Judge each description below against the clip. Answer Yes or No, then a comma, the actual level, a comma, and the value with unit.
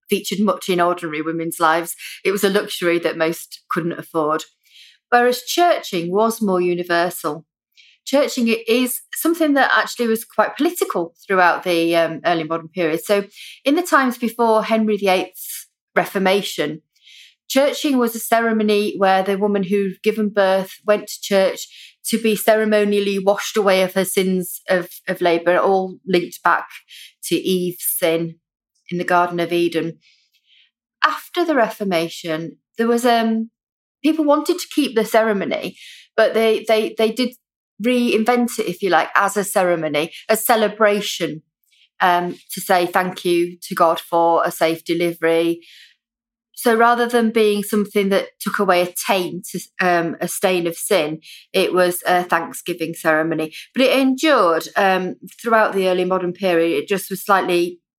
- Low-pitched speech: No, high, 190 Hz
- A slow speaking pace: No, average, 150 wpm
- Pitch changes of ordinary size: Yes, average, 4.6 semitones